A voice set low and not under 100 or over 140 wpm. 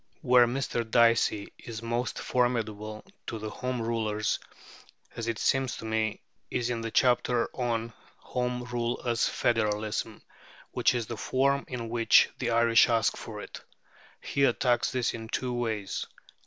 No: low, 115 Hz; average, 150 wpm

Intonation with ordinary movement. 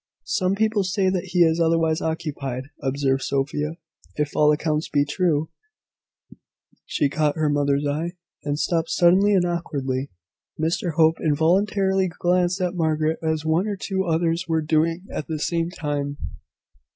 Yes: average, 3.0 semitones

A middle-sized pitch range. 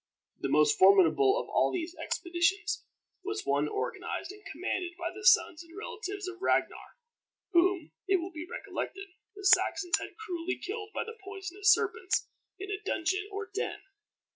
No: narrow, 2.3 semitones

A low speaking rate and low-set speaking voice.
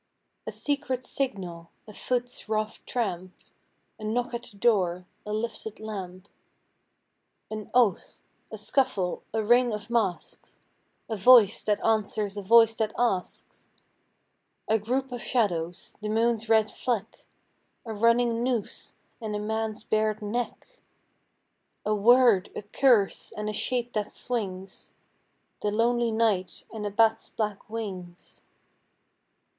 No: slow, 130 wpm; high, 220 Hz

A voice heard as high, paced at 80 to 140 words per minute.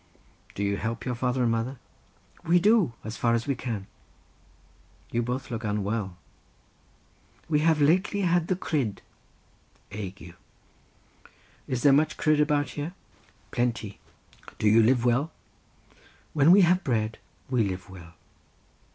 No: low, 125 Hz; slow, 135 wpm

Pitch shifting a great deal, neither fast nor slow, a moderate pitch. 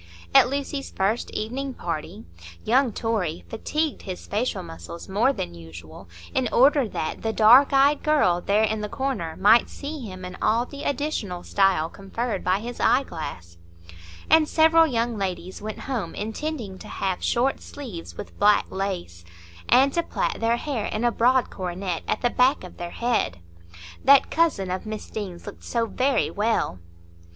No: wide, 6.3 semitones; average, 160 wpm; high, 215 Hz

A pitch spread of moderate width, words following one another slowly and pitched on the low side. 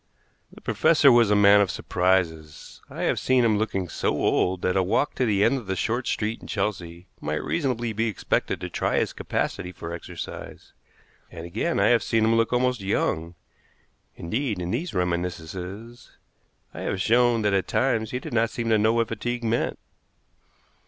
No: average, 4.5 semitones; average, 185 wpm; low, 105 Hz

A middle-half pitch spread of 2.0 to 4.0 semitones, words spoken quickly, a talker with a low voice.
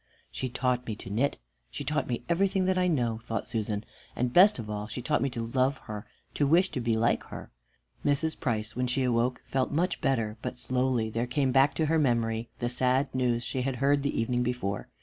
Yes: average, 3.4 semitones; fast, 220 wpm; low, 125 Hz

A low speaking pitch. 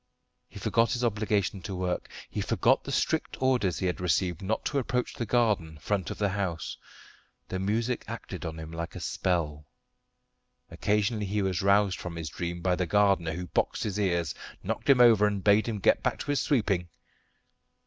Yes: low, 100 Hz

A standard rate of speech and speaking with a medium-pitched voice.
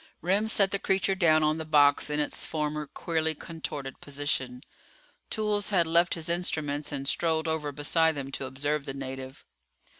Yes: average, 170 wpm; medium, 155 Hz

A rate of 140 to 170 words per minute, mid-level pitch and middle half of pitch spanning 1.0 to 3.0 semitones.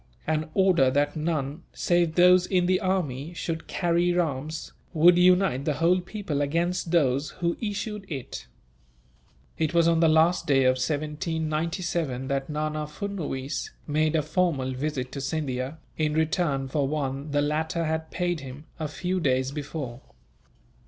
No: average, 150 wpm; medium, 155 Hz; average, 3.6 semitones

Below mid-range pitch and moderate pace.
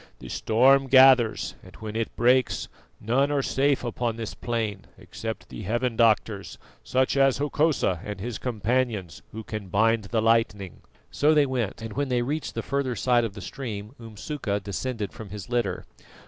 Yes: low, 115 Hz; average, 170 wpm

